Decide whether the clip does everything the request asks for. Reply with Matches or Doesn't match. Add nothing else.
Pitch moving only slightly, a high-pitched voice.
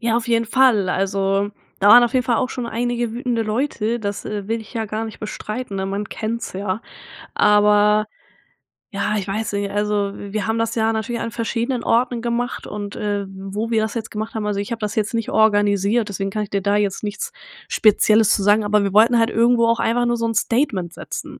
Matches